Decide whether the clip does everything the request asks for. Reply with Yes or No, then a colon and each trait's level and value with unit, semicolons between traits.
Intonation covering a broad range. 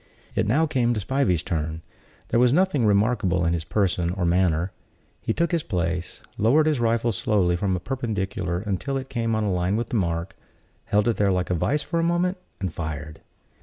Yes: wide, 5.7 semitones